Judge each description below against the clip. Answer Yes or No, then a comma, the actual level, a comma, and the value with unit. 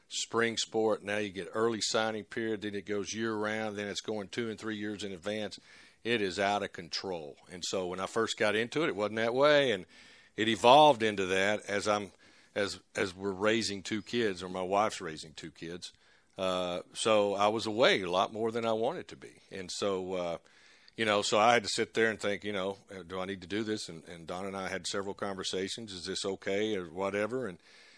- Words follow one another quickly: Yes, fast, 225 wpm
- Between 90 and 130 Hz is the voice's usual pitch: Yes, low, 105 Hz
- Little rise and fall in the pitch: Yes, narrow, 2.3 semitones